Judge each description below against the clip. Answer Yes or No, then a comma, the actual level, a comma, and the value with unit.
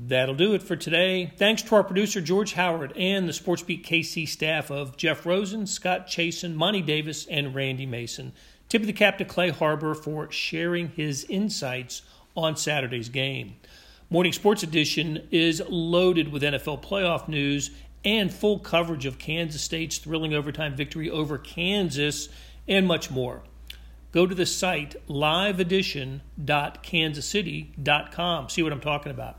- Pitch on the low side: No, medium, 160 Hz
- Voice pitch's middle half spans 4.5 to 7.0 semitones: No, average, 3.7 semitones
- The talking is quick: No, average, 150 wpm